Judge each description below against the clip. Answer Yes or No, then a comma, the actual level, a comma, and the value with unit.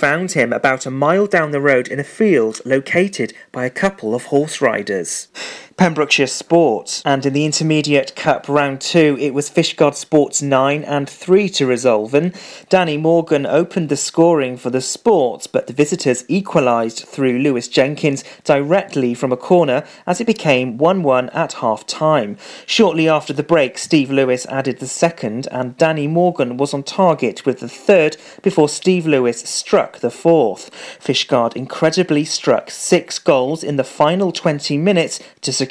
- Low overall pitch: No, medium, 145 Hz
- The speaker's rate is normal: Yes, average, 165 wpm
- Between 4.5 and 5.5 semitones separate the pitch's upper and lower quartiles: No, average, 3.8 semitones